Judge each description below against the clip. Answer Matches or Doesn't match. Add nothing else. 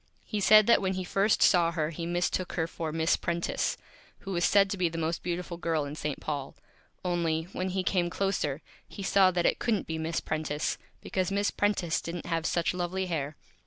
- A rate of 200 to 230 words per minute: Matches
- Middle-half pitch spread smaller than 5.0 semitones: Matches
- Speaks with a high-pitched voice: Doesn't match